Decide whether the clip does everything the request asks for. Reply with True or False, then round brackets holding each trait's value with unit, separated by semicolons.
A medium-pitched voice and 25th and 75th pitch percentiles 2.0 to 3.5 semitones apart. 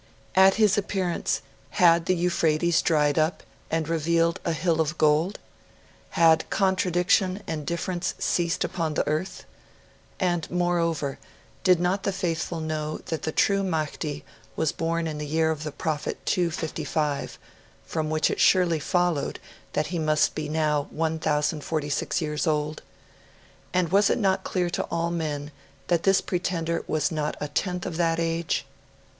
True (165 Hz; 2.5 semitones)